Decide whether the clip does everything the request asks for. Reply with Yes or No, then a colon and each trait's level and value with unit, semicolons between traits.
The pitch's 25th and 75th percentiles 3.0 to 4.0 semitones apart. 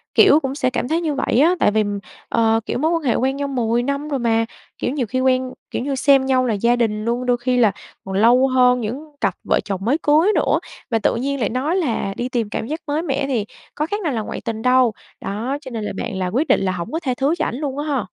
Yes: average, 3.6 semitones